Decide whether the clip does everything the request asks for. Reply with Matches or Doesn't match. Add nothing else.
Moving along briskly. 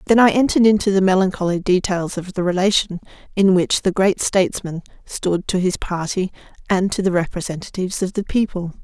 Doesn't match